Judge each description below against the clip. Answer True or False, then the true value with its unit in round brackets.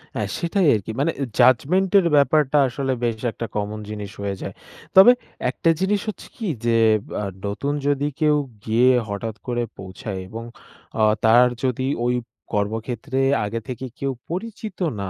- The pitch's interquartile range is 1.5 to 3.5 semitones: False (5.6 semitones)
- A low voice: True (125 Hz)